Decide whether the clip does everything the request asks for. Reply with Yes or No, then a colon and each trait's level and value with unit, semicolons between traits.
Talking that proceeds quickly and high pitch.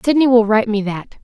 Yes: fast, 245 wpm; high, 225 Hz